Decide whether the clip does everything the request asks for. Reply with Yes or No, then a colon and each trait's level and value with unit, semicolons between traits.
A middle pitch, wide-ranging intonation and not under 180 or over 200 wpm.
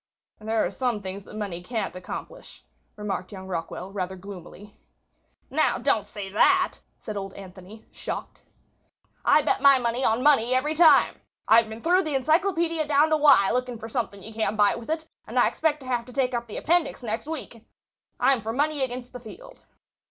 No: high, 235 Hz; wide, 6.1 semitones; average, 190 wpm